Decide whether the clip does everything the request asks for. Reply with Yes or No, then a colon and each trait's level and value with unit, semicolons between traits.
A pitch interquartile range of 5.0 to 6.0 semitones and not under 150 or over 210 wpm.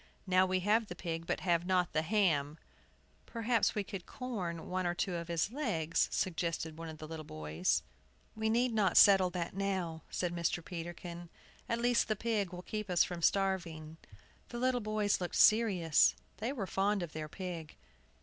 No: average, 4.0 semitones; average, 180 wpm